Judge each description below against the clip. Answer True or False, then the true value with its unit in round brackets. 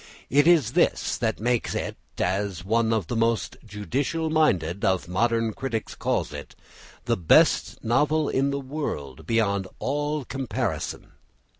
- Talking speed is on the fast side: False (140 wpm)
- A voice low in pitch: True (115 Hz)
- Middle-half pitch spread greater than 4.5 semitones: True (5.6 semitones)